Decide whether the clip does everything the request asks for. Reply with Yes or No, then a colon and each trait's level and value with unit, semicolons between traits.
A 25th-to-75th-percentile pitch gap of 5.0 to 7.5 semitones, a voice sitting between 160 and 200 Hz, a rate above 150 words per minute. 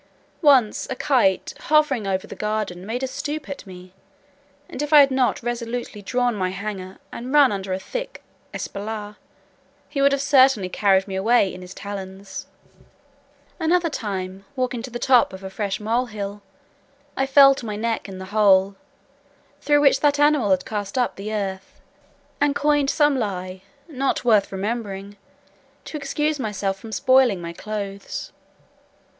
No: wide, 5.5 semitones; high, 215 Hz; average, 160 wpm